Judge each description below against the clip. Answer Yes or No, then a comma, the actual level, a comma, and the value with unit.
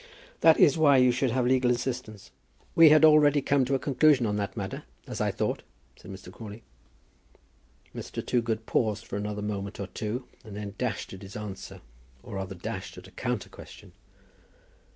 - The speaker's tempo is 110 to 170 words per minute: No, average, 180 wpm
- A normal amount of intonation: Yes, average, 4.3 semitones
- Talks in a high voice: No, low, 115 Hz